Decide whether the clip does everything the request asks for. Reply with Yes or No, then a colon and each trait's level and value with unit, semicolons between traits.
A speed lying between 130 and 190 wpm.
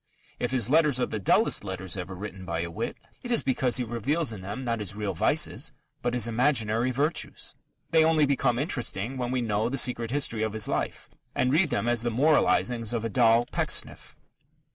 No: fast, 205 wpm